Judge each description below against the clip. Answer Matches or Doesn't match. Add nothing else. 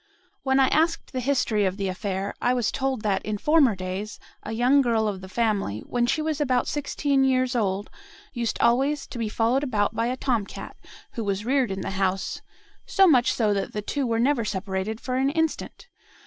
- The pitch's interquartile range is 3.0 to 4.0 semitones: Doesn't match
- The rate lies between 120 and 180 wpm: Doesn't match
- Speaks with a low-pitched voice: Doesn't match